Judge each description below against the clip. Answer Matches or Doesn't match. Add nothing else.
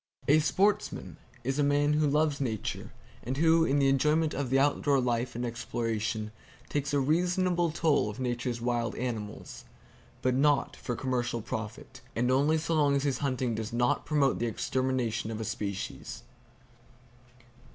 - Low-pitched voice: Matches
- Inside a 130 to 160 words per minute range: Matches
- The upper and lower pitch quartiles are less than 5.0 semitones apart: Matches